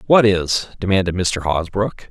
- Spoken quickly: No, average, 145 wpm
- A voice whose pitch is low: Yes, very low, 95 Hz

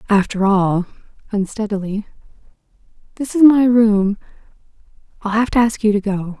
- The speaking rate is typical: No, slow, 115 wpm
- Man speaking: No, female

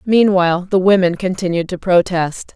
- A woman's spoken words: Yes, female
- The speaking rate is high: No, average, 140 wpm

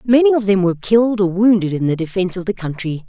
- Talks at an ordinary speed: No, fast, 255 wpm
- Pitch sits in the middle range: No, high, 195 Hz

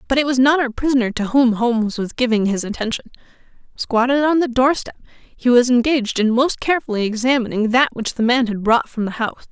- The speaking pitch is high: Yes, high, 245 Hz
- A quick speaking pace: Yes, fast, 210 wpm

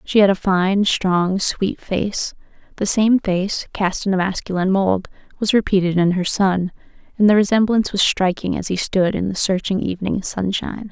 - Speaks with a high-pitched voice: Yes, high, 195 Hz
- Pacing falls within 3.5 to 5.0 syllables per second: Yes, 4.9 syllables/s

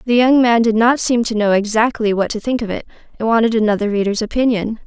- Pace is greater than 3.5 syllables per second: Yes, 6.2 syllables/s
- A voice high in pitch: Yes, high, 225 Hz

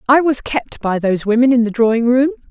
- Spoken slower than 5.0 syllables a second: No, 6.0 syllables/s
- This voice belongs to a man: No, female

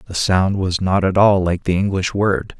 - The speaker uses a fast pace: Yes, fast, 230 wpm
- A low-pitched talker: Yes, very low, 95 Hz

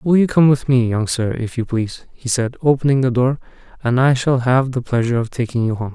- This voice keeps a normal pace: No, fast, 250 wpm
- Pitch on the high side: No, low, 125 Hz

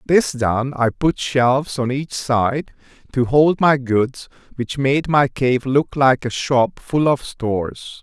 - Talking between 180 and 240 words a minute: No, average, 170 wpm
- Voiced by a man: Yes, male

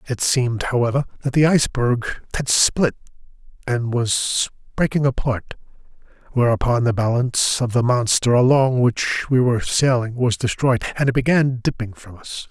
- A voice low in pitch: Yes, low, 125 Hz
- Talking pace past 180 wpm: No, average, 150 wpm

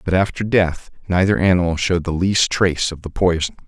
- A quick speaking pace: No, average, 195 wpm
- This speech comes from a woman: No, male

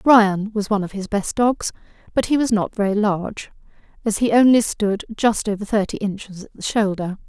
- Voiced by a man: No, female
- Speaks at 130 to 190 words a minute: No, average, 200 wpm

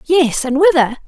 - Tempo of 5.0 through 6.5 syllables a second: No, 4.5 syllables/s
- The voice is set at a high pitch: Yes, very high, 300 Hz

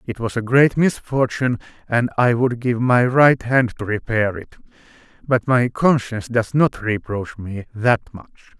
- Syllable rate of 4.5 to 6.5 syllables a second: No, 4.3 syllables/s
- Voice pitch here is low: Yes, low, 120 Hz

